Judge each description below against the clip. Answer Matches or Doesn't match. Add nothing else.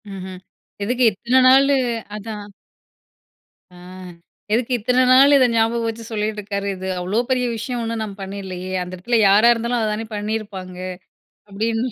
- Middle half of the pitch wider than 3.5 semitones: Doesn't match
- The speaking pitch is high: Matches